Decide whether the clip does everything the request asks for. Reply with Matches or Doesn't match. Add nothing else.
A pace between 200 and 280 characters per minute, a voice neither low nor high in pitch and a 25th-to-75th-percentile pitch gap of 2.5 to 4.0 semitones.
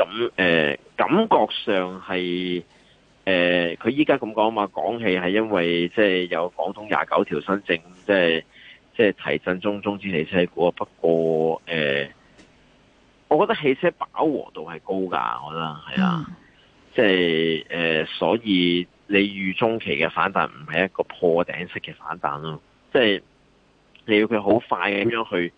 Doesn't match